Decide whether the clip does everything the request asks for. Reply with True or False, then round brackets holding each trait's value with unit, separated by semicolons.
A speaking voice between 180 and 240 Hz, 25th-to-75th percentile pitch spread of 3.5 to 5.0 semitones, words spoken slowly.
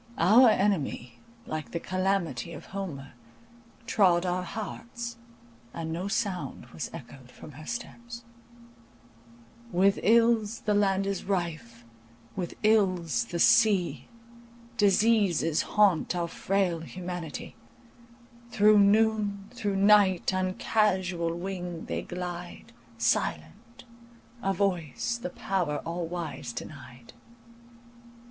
True (185 Hz; 3.9 semitones; 105 wpm)